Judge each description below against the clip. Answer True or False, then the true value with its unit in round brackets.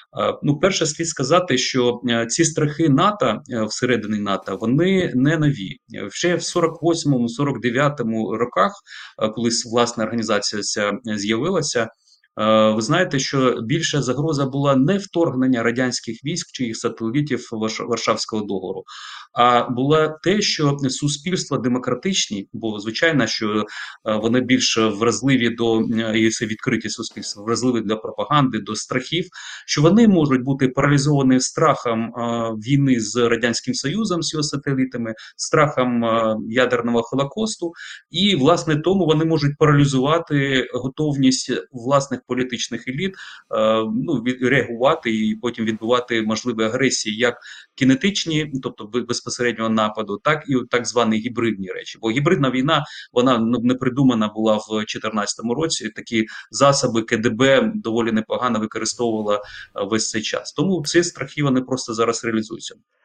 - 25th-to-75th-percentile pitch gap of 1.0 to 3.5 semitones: False (4.3 semitones)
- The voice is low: True (125 Hz)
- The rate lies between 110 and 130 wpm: True (125 wpm)